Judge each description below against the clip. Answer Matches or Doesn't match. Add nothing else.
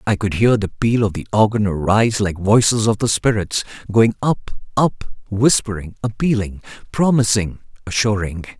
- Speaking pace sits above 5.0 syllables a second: Doesn't match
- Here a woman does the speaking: Doesn't match